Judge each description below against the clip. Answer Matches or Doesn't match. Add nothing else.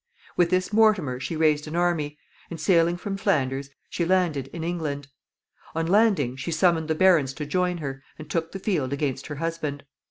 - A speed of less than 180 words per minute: Doesn't match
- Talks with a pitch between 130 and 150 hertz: Doesn't match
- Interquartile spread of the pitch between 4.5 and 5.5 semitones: Doesn't match